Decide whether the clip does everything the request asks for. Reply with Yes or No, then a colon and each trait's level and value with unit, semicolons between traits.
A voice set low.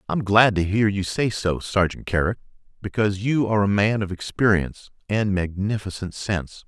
Yes: low, 100 Hz